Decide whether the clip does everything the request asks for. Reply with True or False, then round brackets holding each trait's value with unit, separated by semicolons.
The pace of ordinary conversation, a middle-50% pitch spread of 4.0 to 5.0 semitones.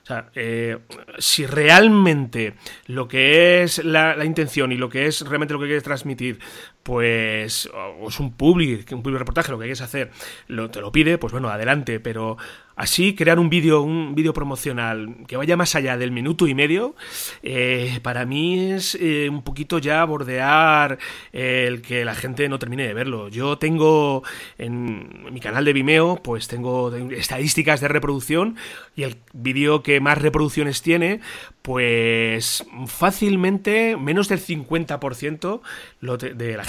True (165 wpm; 4.3 semitones)